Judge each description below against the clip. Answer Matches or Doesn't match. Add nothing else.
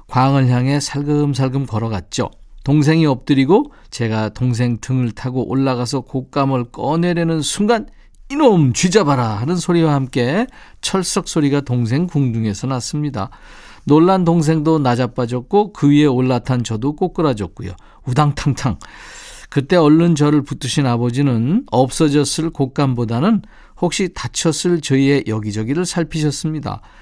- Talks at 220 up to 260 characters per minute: Doesn't match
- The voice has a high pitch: Doesn't match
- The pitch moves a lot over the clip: Doesn't match